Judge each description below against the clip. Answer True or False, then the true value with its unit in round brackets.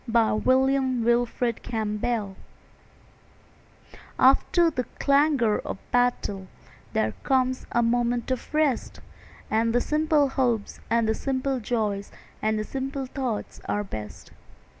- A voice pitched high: True (245 Hz)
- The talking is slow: True (115 wpm)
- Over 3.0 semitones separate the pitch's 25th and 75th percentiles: True (3.4 semitones)